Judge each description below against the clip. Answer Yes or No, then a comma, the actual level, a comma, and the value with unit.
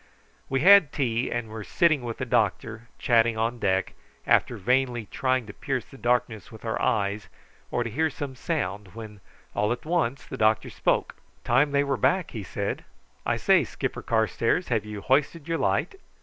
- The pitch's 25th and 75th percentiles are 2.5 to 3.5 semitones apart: No, average, 4.1 semitones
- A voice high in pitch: No, low, 120 Hz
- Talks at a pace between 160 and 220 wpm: Yes, average, 180 wpm